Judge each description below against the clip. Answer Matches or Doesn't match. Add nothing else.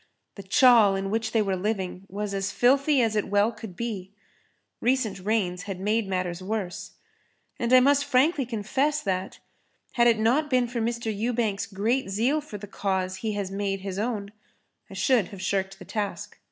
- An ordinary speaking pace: Matches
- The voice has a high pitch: Matches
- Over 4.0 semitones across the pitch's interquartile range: Doesn't match